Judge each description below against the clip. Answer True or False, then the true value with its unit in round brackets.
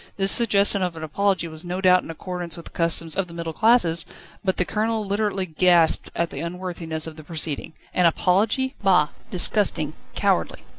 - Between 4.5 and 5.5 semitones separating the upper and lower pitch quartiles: False (3.1 semitones)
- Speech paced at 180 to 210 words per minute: True (185 wpm)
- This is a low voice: False (180 Hz)